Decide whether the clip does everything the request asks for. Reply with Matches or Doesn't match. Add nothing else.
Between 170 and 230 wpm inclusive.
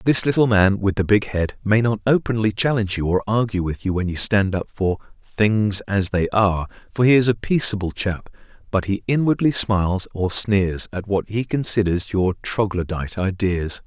Matches